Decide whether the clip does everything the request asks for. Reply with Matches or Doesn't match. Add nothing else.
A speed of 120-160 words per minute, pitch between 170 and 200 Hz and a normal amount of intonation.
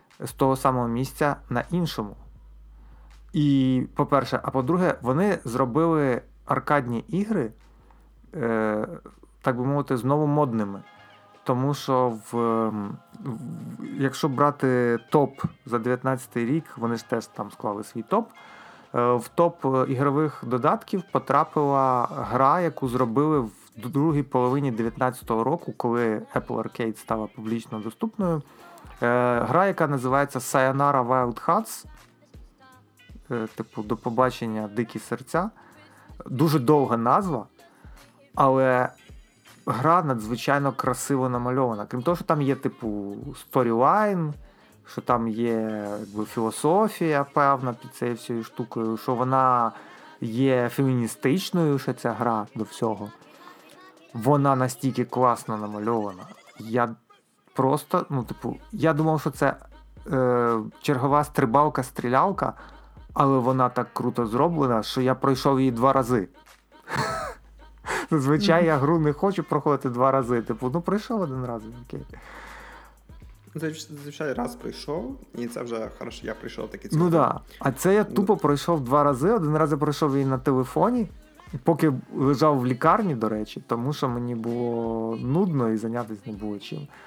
Doesn't match